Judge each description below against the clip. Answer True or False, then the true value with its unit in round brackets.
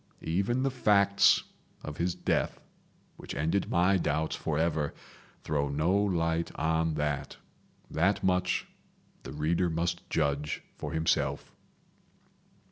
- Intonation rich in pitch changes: False (3.0 semitones)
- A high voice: False (80 Hz)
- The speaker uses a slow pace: True (115 wpm)